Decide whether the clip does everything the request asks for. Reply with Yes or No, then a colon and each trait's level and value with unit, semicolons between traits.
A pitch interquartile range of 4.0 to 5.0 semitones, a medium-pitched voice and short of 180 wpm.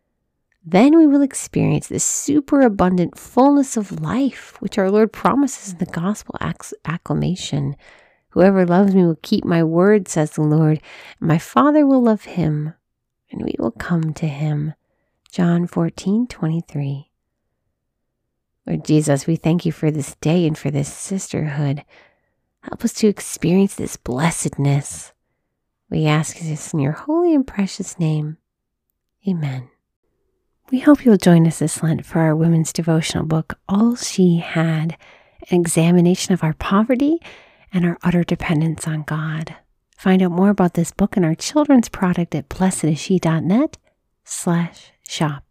Yes: average, 4.3 semitones; medium, 175 Hz; average, 150 wpm